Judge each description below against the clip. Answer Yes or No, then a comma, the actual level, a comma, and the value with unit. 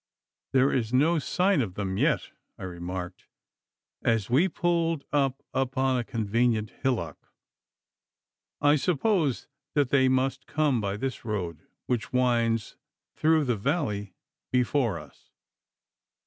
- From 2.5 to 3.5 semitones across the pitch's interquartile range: No, average, 5.1 semitones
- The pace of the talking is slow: Yes, slow, 120 wpm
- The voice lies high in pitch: No, low, 125 Hz